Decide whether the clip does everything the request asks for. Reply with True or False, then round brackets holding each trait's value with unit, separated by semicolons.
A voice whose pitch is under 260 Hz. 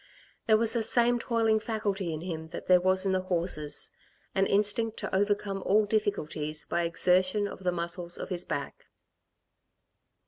True (190 Hz)